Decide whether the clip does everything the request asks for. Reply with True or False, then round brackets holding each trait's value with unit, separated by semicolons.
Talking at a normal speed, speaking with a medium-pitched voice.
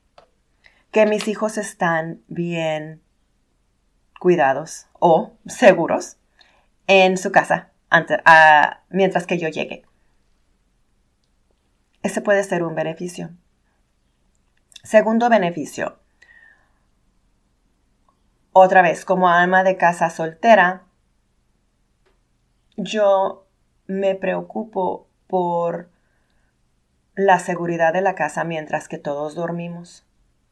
False (85 wpm; 170 Hz)